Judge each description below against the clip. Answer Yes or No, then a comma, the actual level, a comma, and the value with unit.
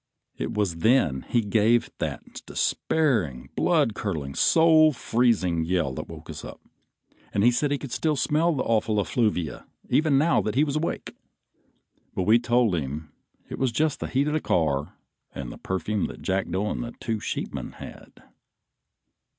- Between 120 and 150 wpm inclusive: No, average, 165 wpm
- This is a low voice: Yes, low, 110 Hz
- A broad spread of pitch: Yes, wide, 7.7 semitones